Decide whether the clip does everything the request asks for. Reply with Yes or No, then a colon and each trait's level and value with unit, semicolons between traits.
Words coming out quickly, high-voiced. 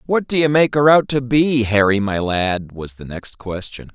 No: fast, 215 wpm; low, 120 Hz